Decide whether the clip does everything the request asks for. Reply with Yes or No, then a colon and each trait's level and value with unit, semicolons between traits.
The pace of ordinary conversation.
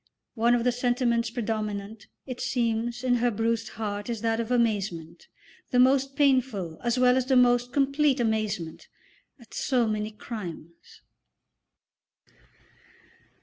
No: slow, 130 wpm